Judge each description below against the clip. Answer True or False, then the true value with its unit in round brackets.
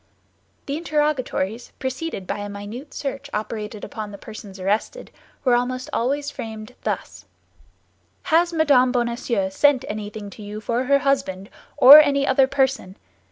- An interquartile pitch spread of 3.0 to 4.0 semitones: False (4.9 semitones)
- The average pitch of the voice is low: False (250 Hz)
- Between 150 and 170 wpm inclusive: False (140 wpm)